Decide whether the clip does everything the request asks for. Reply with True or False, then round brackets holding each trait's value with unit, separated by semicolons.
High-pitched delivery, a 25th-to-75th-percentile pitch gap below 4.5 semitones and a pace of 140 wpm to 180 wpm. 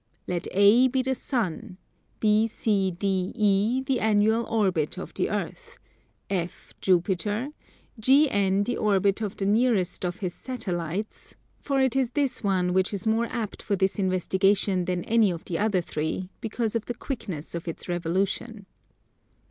True (205 Hz; 3.7 semitones; 150 wpm)